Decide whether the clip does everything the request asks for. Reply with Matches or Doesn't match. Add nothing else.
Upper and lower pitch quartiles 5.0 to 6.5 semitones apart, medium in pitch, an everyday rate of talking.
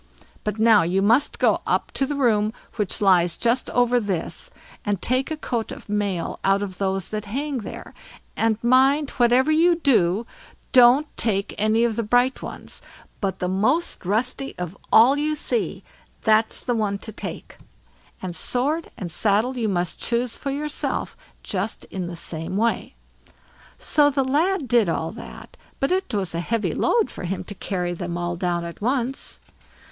Doesn't match